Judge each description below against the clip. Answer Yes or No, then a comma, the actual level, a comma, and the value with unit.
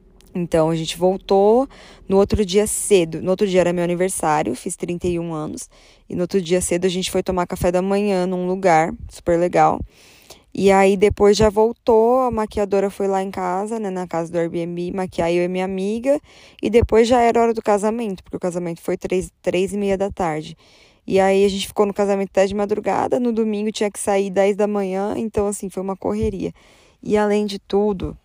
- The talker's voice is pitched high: Yes, high, 195 Hz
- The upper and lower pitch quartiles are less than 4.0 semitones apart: Yes, narrow, 2.4 semitones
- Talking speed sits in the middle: No, fast, 210 wpm